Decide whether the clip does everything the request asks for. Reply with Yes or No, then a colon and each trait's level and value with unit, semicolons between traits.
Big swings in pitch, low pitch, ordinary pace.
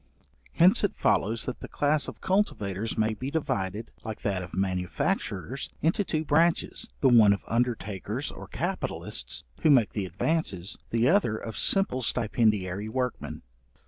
Yes: wide, 5.9 semitones; low, 115 Hz; average, 145 wpm